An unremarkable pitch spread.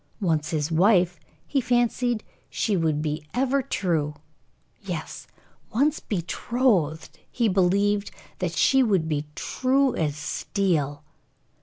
No: wide, 7.4 semitones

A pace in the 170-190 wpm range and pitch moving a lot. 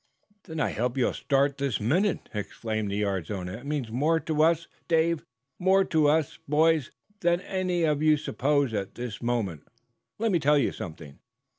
Yes: average, 175 wpm; wide, 6.4 semitones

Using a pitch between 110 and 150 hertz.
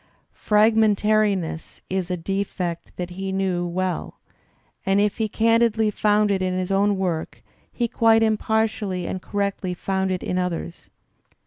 No: high, 195 Hz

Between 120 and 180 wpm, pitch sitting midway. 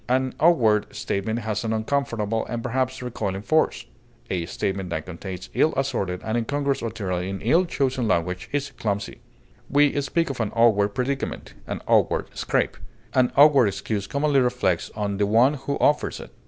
No: average, 165 wpm; low, 115 Hz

